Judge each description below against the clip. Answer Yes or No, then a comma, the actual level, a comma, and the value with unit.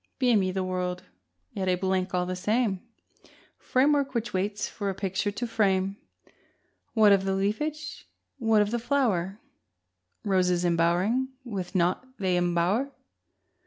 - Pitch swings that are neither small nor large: Yes, average, 3.8 semitones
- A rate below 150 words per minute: Yes, slow, 135 wpm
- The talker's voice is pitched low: No, high, 195 Hz